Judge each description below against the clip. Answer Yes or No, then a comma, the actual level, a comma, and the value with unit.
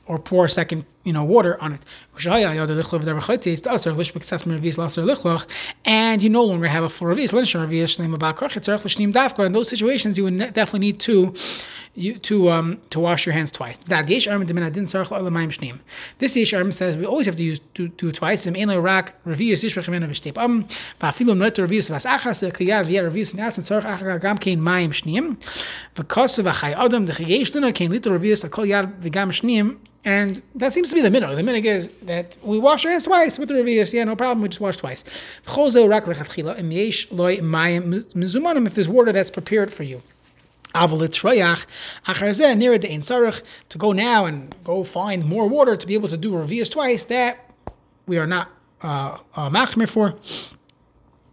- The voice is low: No, high, 195 Hz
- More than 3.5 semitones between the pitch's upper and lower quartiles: Yes, average, 4.6 semitones